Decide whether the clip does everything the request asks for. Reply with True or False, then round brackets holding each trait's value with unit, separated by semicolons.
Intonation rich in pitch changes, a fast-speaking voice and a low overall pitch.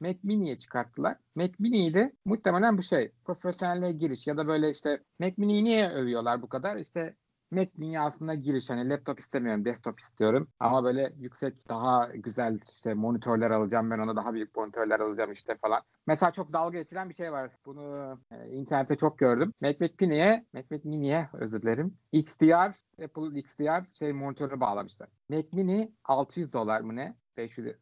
False (6.2 semitones; 175 wpm; 145 Hz)